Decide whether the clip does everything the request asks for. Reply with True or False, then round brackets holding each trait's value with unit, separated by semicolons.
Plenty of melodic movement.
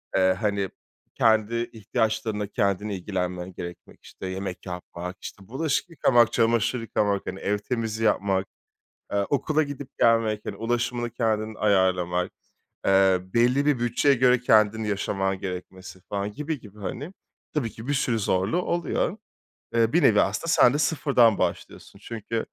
False (3.8 semitones)